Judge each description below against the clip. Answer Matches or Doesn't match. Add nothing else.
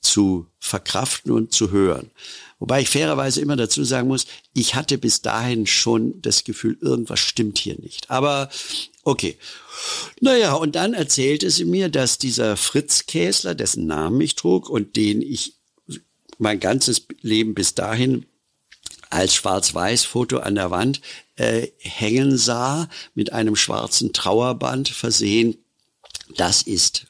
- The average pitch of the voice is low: Matches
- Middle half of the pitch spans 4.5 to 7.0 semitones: Doesn't match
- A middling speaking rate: Matches